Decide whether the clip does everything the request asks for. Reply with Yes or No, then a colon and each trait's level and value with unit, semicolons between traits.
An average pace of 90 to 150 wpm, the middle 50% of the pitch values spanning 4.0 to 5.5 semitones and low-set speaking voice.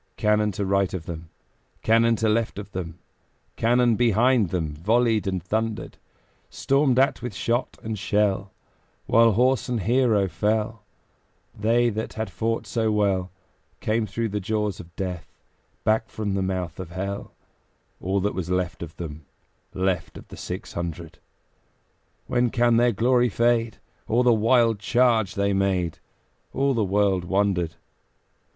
No: average, 145 wpm; average, 3.6 semitones; low, 105 Hz